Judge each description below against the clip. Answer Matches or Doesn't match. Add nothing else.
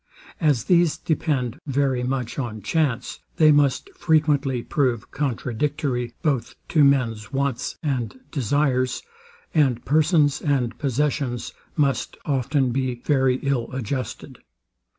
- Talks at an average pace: Doesn't match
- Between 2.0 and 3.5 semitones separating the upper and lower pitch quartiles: Matches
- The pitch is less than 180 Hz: Matches